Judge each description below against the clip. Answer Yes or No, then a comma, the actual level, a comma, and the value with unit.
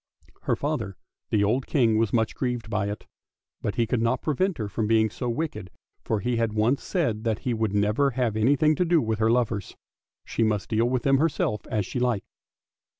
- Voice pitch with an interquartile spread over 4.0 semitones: No, average, 3.2 semitones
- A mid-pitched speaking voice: No, low, 115 Hz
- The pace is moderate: No, fast, 210 wpm